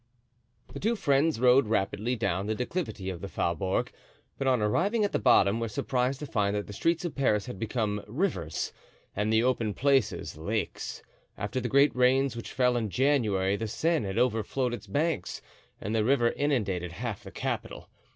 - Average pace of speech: Yes, average, 180 wpm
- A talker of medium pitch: No, low, 115 Hz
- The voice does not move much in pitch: No, average, 4.8 semitones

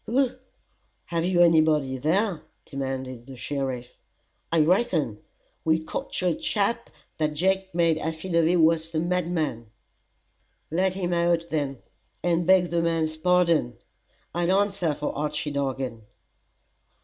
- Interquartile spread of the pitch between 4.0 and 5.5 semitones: No, average, 3.3 semitones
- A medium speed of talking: No, slow, 125 wpm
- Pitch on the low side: No, medium, 165 Hz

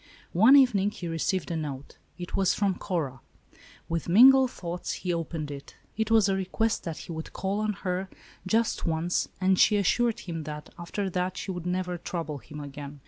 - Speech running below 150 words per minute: No, average, 190 wpm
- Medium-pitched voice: Yes, medium, 180 Hz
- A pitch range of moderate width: Yes, average, 3.7 semitones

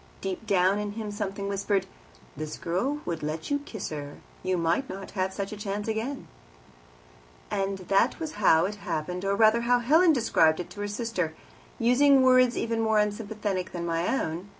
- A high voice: Yes, high, 205 Hz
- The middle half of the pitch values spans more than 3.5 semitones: Yes, average, 4.0 semitones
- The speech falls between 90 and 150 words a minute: No, average, 175 wpm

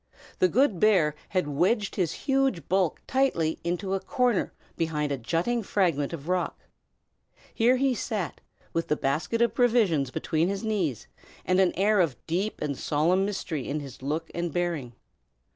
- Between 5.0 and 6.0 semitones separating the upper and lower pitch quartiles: Yes, wide, 5.5 semitones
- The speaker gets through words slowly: No, average, 160 wpm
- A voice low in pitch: No, medium, 180 Hz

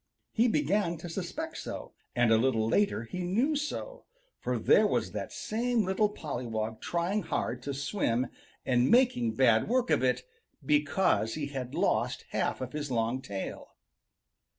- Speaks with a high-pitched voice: No, medium, 150 Hz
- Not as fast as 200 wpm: Yes, average, 155 wpm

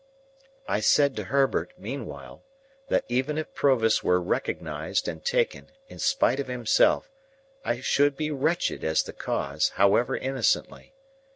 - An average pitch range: Yes, average, 4.8 semitones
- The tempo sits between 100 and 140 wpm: Yes, slow, 135 wpm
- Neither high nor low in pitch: No, low, 130 Hz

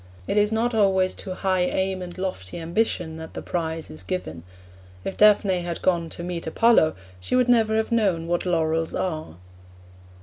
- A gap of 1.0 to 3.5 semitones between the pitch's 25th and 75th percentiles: No, average, 4.0 semitones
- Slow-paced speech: No, average, 175 wpm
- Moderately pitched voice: Yes, medium, 180 Hz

